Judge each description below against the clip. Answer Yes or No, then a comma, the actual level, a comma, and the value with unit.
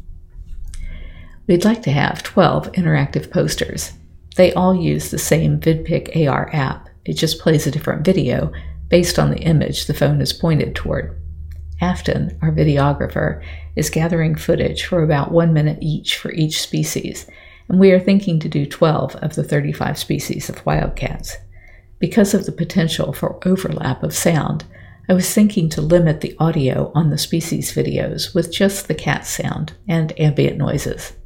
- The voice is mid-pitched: Yes, medium, 155 Hz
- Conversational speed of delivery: Yes, average, 160 wpm